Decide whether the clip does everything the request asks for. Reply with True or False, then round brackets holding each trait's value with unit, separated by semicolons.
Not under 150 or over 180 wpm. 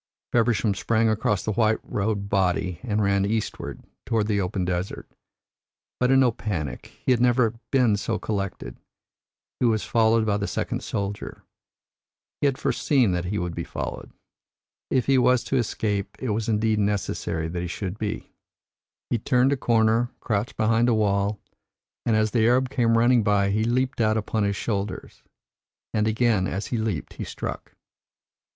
True (170 wpm)